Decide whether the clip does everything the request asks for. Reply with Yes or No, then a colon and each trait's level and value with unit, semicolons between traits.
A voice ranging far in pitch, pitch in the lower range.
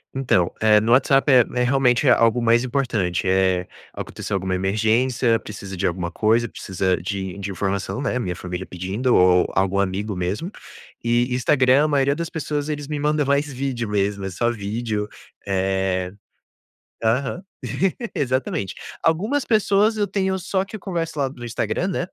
Yes: wide, 6.5 semitones; low, 120 Hz